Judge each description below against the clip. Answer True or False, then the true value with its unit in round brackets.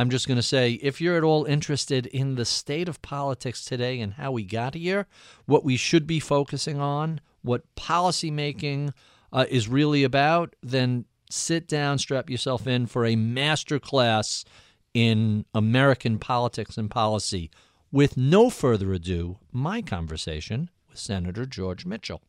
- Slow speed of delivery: False (155 wpm)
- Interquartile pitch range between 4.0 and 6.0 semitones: True (4.4 semitones)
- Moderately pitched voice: False (130 Hz)